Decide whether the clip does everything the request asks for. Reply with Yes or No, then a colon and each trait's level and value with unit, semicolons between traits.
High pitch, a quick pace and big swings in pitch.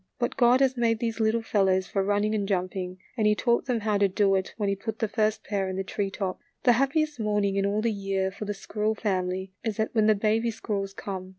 No: high, 210 Hz; fast, 250 wpm; narrow, 2.4 semitones